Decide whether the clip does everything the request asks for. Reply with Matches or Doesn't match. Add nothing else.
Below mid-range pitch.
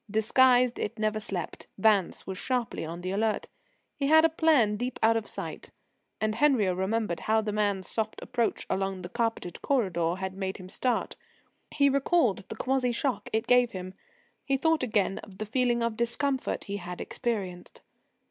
Doesn't match